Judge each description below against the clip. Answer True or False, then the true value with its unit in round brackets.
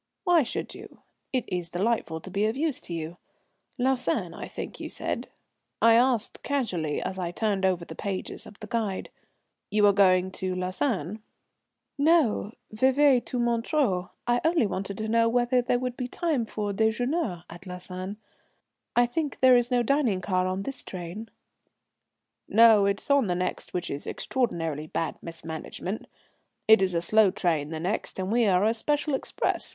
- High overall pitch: True (215 Hz)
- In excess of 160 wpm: True (175 wpm)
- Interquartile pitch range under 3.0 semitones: False (5.1 semitones)